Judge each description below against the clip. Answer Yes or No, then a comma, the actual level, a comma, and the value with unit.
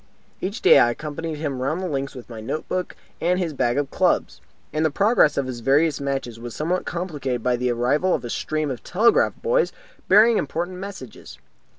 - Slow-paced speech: No, average, 200 wpm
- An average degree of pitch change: No, wide, 6.0 semitones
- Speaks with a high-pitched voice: No, medium, 150 Hz